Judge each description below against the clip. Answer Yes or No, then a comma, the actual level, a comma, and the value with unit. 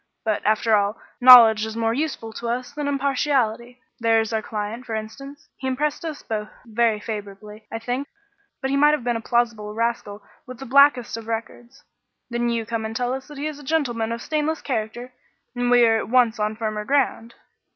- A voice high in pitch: Yes, high, 235 Hz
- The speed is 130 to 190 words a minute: No, fast, 205 wpm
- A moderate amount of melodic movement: Yes, average, 3.2 semitones